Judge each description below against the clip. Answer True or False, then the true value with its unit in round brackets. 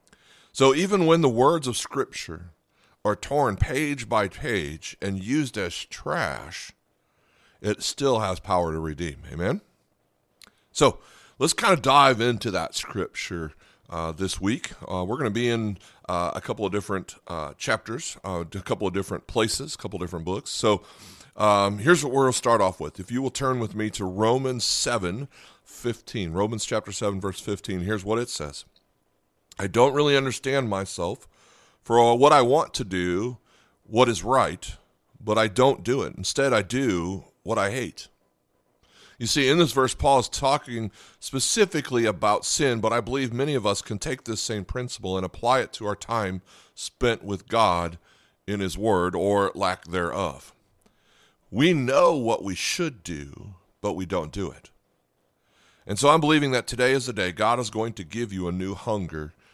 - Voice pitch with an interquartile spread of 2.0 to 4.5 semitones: False (5.2 semitones)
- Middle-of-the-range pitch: False (110 Hz)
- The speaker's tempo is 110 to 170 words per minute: False (180 wpm)